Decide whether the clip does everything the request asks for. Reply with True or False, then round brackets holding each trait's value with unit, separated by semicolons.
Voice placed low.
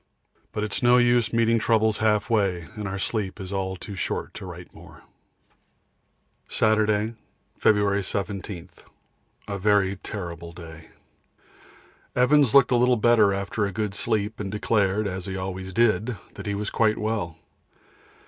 True (105 Hz)